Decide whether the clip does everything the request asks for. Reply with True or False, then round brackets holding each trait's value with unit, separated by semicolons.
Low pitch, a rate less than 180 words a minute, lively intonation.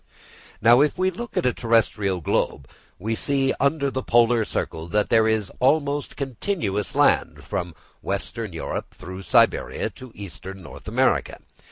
True (115 Hz; 145 wpm; 5.9 semitones)